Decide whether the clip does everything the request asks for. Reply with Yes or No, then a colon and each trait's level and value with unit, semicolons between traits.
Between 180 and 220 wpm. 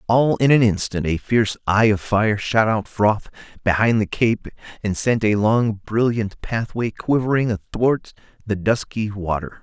No: average, 160 wpm